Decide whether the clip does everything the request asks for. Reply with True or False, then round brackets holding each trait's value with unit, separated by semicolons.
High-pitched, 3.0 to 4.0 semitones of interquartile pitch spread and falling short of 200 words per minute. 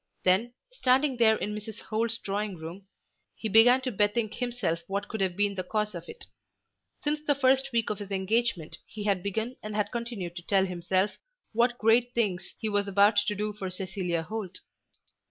True (210 Hz; 3.5 semitones; 190 wpm)